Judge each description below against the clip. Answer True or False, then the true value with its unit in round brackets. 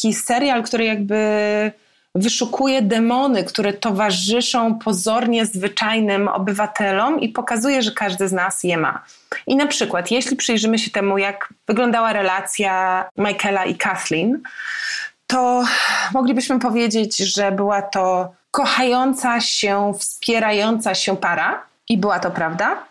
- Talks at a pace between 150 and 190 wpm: False (120 wpm)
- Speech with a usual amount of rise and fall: True (3.6 semitones)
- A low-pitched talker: False (215 Hz)